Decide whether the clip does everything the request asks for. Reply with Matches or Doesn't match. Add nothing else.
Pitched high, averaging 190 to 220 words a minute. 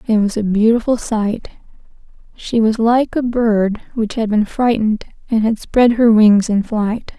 Doesn't match